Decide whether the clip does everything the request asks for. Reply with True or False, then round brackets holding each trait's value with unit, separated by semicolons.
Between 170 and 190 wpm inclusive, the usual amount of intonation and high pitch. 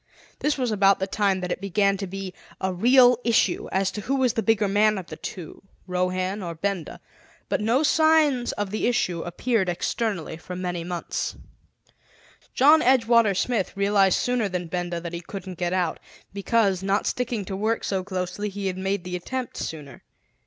True (180 wpm; 4.0 semitones; 195 Hz)